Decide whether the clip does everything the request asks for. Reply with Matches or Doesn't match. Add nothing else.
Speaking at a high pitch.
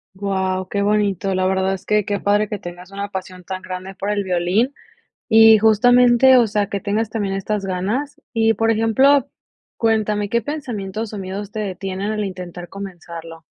Matches